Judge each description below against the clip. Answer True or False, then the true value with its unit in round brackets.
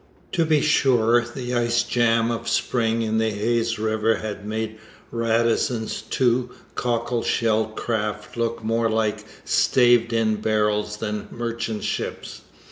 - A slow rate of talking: True (130 wpm)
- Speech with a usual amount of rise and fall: False (1.4 semitones)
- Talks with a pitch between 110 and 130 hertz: True (115 Hz)